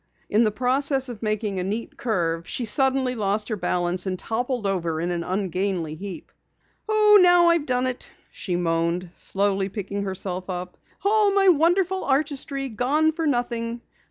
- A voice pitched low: No, high, 220 Hz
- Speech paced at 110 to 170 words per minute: Yes, average, 160 wpm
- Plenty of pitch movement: Yes, wide, 6.6 semitones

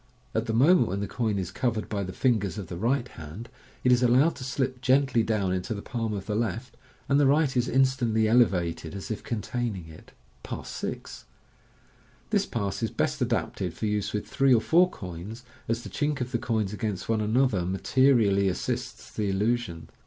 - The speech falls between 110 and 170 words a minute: No, average, 200 wpm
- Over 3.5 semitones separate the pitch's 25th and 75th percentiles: Yes, average, 4.3 semitones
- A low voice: Yes, low, 110 Hz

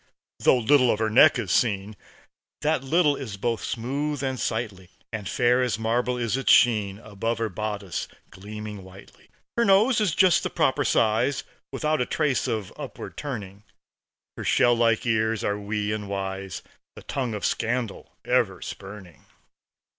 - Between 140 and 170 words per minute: Yes, average, 160 wpm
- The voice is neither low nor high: No, low, 115 Hz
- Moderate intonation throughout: Yes, average, 4.2 semitones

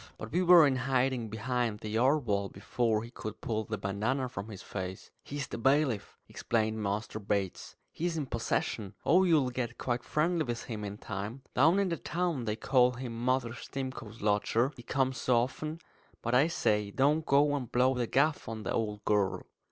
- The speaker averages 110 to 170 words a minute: No, average, 190 wpm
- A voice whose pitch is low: Yes, low, 120 Hz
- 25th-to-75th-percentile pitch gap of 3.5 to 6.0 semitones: Yes, average, 4.1 semitones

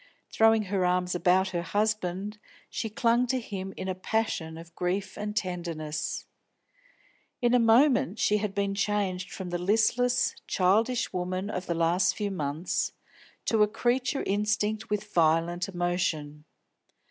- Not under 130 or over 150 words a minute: Yes, average, 145 wpm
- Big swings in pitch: No, average, 3.4 semitones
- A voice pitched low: No, high, 195 Hz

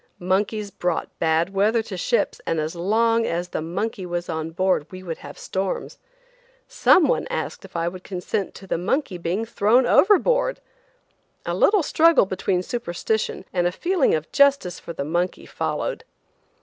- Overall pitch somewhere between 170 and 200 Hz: Yes, high, 190 Hz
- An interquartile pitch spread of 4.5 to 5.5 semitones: Yes, average, 4.8 semitones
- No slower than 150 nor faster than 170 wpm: Yes, average, 165 wpm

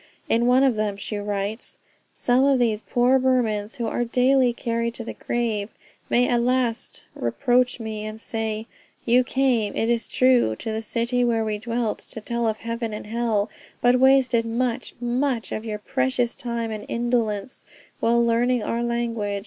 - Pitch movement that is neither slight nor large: No, narrow, 2.0 semitones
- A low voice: No, high, 235 Hz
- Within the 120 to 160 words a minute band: No, average, 175 wpm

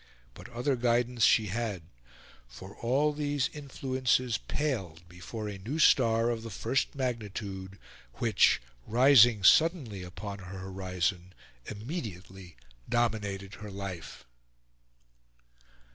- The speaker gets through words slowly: Yes, slow, 105 wpm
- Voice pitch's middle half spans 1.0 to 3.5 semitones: No, average, 4.6 semitones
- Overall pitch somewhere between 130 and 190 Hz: No, low, 110 Hz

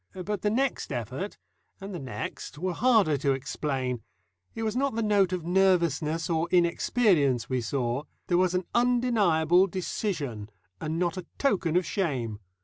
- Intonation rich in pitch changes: Yes, wide, 6.0 semitones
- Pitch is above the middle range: No, medium, 175 Hz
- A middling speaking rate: Yes, average, 155 wpm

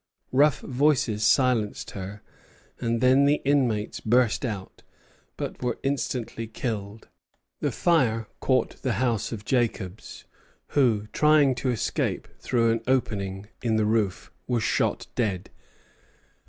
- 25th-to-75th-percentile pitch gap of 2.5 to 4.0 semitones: Yes, average, 3.5 semitones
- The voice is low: Yes, low, 115 Hz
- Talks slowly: Yes, slow, 125 wpm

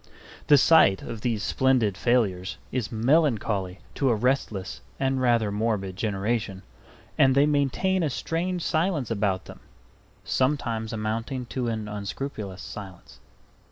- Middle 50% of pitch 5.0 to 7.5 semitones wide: No, average, 4.5 semitones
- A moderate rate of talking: No, slow, 125 wpm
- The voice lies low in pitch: Yes, low, 115 Hz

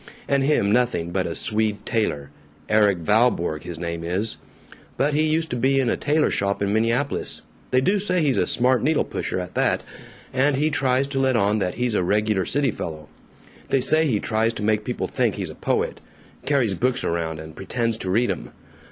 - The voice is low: Yes, low, 115 Hz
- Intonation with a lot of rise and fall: Yes, wide, 5.7 semitones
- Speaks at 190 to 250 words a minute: Yes, fast, 205 wpm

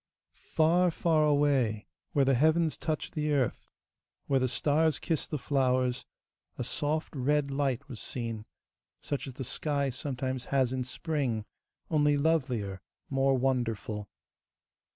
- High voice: No, low, 135 Hz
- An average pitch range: Yes, average, 3.0 semitones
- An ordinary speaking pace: No, slow, 130 wpm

